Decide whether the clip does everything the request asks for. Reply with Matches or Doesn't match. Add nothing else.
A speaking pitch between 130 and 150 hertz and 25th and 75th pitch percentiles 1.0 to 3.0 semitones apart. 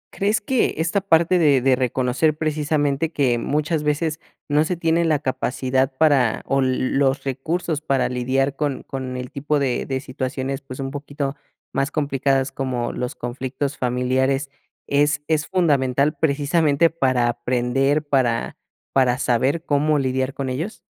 Matches